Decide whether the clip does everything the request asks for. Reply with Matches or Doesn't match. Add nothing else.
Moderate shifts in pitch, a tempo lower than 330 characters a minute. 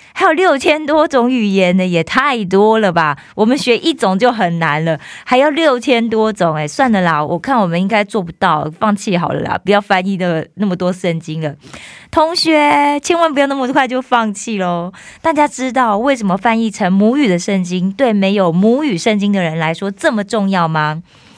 Doesn't match